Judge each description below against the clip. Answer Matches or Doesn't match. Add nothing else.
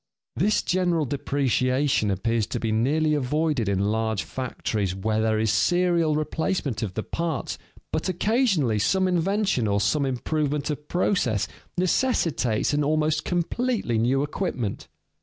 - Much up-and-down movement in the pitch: Matches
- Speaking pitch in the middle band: Matches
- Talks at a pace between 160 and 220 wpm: Doesn't match